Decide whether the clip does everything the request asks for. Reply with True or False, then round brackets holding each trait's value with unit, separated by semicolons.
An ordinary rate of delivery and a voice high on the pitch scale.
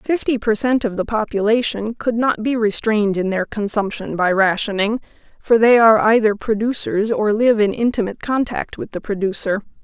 True (170 wpm; 215 Hz)